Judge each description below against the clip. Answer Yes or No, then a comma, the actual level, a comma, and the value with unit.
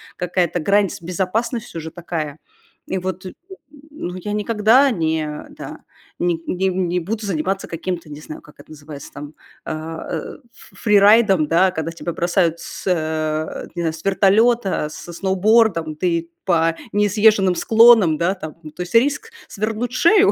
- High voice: No, medium, 180 Hz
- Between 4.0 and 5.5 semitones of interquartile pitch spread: Yes, average, 4.3 semitones